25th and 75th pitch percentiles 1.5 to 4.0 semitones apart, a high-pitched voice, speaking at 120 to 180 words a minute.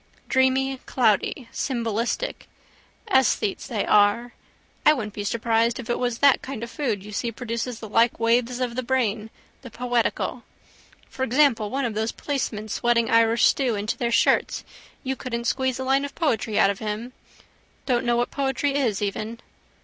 Yes: average, 2.9 semitones; high, 235 Hz; average, 170 wpm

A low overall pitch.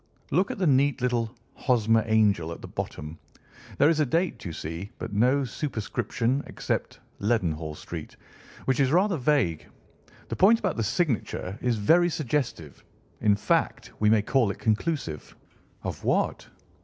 Yes: low, 120 Hz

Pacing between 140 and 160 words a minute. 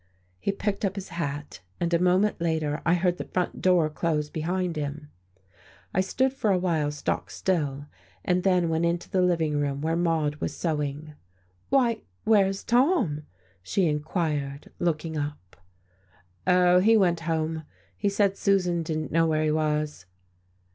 Yes: average, 155 wpm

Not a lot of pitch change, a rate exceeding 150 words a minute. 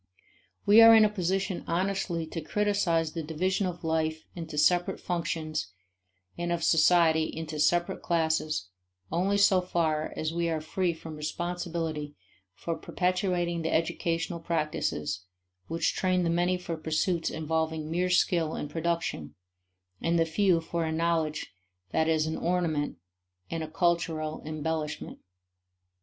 No: narrow, 2.0 semitones; average, 140 wpm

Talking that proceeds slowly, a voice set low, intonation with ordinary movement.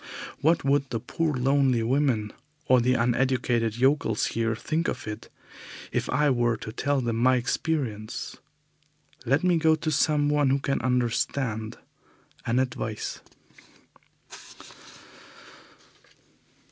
Yes: slow, 115 wpm; low, 130 Hz; average, 3.7 semitones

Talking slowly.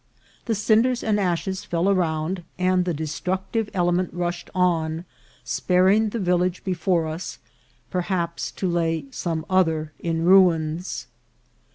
Yes: slow, 130 wpm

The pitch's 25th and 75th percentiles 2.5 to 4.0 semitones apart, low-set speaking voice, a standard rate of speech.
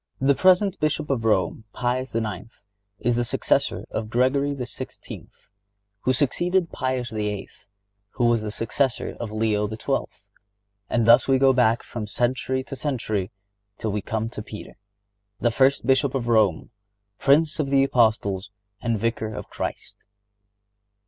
Yes: average, 3.6 semitones; low, 120 Hz; average, 145 wpm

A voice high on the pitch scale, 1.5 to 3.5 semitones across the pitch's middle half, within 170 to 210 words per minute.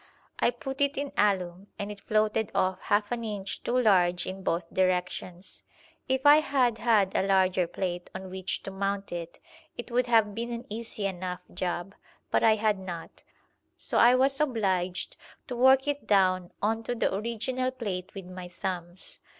No: high, 200 Hz; average, 4.4 semitones; average, 175 wpm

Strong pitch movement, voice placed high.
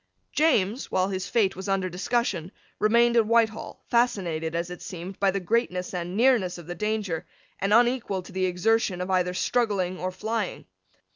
No: average, 3.8 semitones; high, 195 Hz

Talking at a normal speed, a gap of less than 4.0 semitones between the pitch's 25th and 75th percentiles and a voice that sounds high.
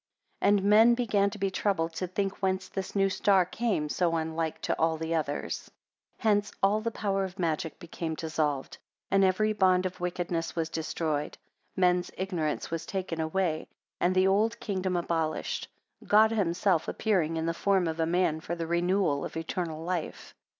No: average, 180 wpm; average, 3.2 semitones; medium, 180 Hz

